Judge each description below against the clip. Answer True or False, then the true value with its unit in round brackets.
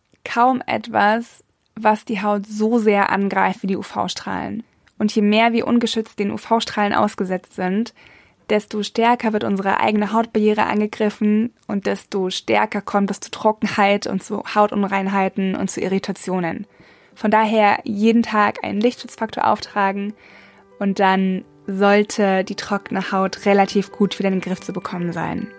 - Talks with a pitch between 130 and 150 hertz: False (205 Hz)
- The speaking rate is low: False (145 wpm)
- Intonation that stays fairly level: True (1.9 semitones)